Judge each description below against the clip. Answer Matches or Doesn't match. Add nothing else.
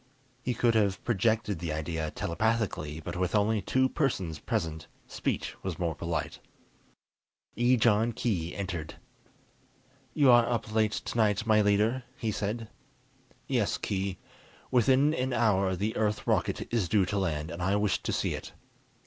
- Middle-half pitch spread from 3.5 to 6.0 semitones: Matches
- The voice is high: Doesn't match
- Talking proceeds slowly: Doesn't match